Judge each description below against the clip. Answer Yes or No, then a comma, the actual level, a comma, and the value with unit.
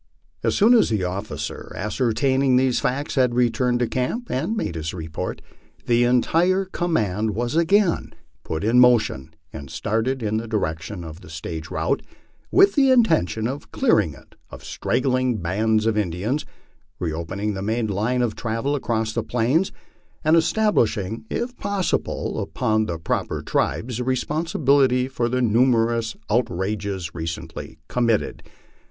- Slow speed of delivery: No, average, 145 wpm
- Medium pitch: No, low, 115 Hz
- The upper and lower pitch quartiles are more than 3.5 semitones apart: Yes, average, 4.3 semitones